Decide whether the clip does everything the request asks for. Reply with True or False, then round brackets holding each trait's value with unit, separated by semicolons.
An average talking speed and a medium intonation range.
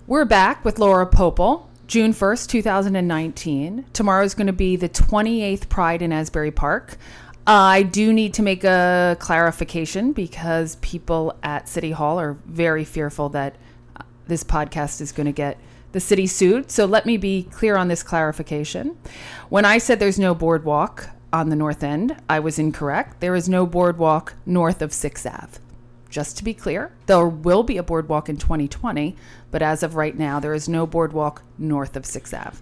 True (180 wpm; 4.2 semitones)